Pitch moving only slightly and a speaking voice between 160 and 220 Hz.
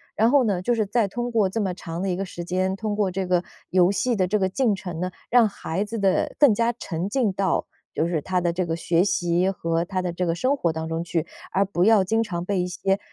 No: average, 3.3 semitones; high, 190 Hz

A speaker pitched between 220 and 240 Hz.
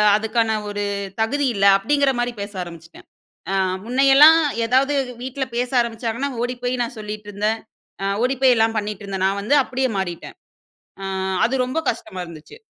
Yes: high, 230 Hz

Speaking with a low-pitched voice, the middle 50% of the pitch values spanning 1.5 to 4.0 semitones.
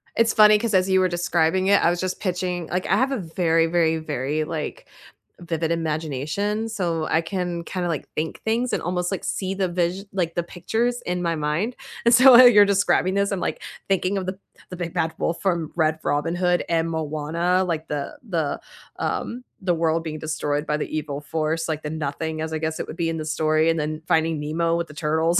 No: medium, 170 Hz; average, 2.9 semitones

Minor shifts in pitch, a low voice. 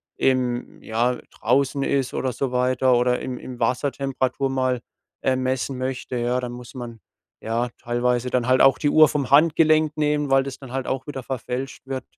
Yes: narrow, 1.6 semitones; low, 130 Hz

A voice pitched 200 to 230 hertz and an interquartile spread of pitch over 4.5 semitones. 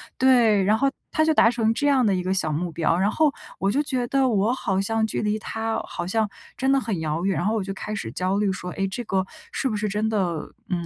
No: high, 210 Hz; average, 4.0 semitones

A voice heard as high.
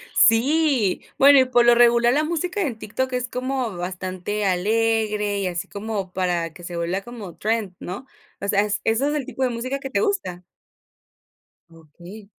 Yes: high, 220 Hz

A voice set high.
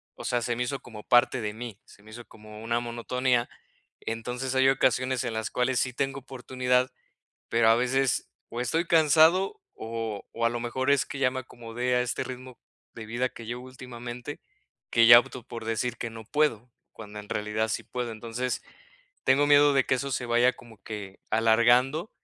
No: low, 120 Hz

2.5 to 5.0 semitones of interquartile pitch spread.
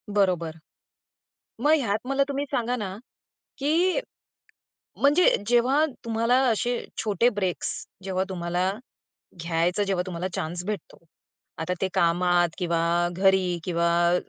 No: wide, 5.6 semitones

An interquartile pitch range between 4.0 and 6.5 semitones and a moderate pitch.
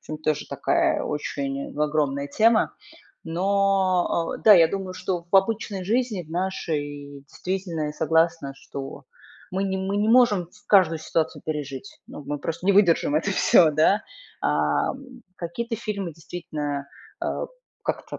Yes: average, 4.6 semitones; medium, 170 Hz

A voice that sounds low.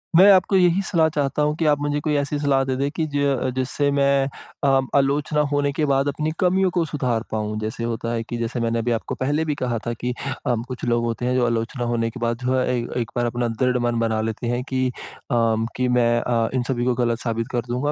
Yes: low, 125 Hz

